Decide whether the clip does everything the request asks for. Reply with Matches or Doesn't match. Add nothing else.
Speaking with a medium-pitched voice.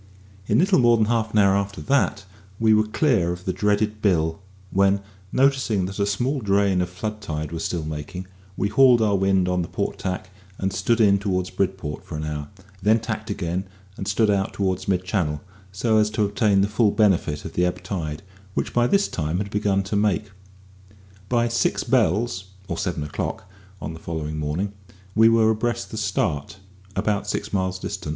Doesn't match